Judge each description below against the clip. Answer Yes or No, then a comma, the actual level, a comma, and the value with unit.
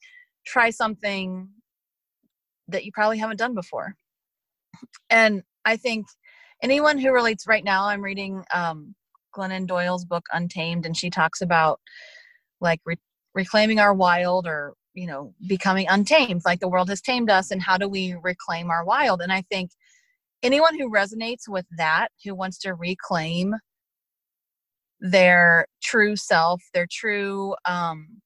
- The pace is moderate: Yes, average, 145 wpm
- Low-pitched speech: No, high, 195 Hz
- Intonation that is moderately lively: Yes, average, 3.9 semitones